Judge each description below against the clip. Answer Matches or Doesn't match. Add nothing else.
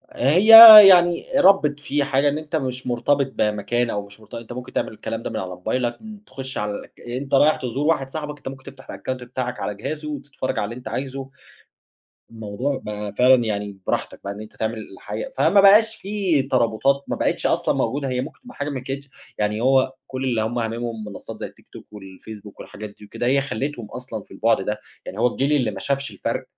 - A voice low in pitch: Matches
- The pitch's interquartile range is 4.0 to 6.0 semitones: Matches